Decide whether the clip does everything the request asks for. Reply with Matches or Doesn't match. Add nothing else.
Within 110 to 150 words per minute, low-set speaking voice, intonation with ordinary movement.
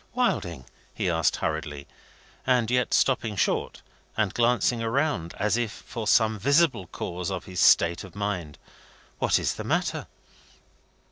Doesn't match